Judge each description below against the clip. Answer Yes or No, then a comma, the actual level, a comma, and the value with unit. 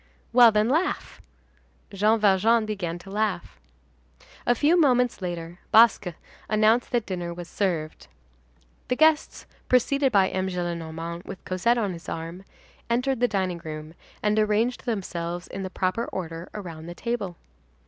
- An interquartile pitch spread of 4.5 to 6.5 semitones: Yes, average, 5.1 semitones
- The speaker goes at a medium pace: Yes, average, 145 wpm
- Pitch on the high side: Yes, high, 195 Hz